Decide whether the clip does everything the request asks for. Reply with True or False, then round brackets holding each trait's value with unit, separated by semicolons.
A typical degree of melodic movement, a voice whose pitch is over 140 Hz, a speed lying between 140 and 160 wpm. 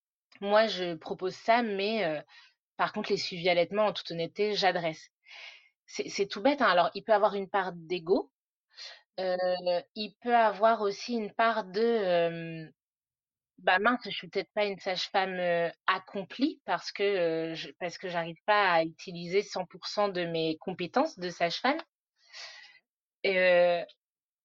True (3.3 semitones; 190 Hz; 150 wpm)